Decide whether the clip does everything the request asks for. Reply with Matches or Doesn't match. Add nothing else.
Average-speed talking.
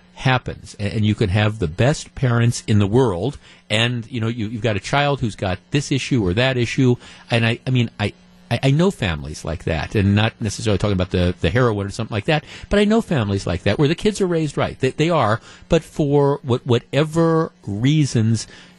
Doesn't match